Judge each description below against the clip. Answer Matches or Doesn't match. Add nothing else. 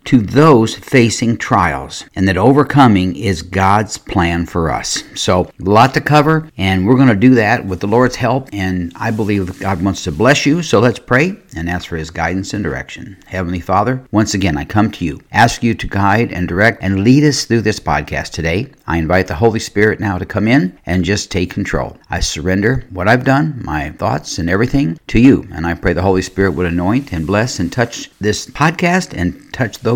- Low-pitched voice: Matches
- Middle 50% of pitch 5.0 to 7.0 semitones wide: Matches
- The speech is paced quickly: Matches